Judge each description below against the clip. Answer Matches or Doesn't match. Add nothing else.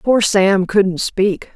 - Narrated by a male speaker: Doesn't match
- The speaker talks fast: Doesn't match